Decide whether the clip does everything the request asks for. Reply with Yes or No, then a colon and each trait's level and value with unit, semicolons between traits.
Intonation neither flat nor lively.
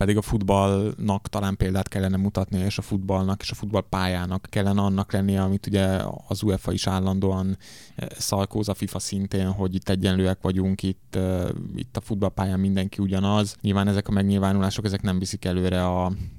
No: narrow, 1.1 semitones